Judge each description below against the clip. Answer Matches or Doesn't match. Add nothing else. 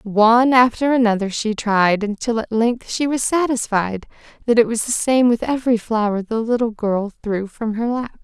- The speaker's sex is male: Doesn't match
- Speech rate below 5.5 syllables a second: Matches